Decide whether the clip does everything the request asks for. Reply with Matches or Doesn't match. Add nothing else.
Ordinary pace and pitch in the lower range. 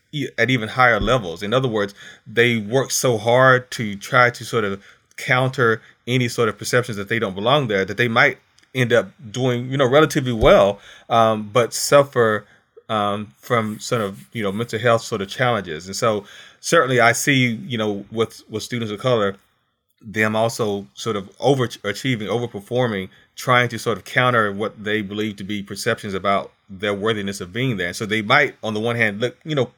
Matches